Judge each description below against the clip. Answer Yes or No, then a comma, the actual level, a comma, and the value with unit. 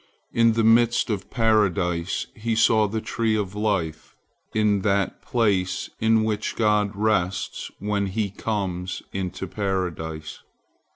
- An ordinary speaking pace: No, slow, 125 wpm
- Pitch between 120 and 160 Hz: No, low, 105 Hz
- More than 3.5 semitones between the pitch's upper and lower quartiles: No, average, 2.8 semitones